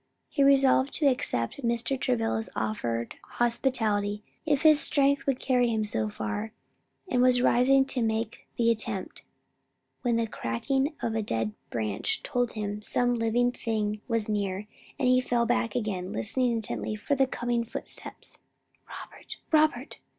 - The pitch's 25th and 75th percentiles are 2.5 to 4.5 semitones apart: Yes, average, 3.7 semitones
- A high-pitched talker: Yes, high, 230 Hz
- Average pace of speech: Yes, average, 150 wpm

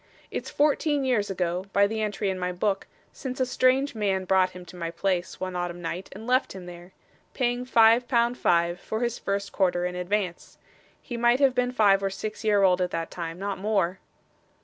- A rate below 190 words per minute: No, fast, 205 wpm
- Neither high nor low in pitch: No, high, 200 Hz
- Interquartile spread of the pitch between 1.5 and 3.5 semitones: No, average, 4.8 semitones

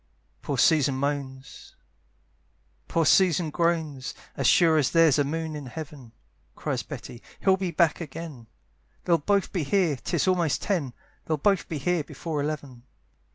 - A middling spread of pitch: Yes, average, 3.3 semitones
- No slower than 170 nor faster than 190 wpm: No, average, 150 wpm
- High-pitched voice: No, medium, 155 Hz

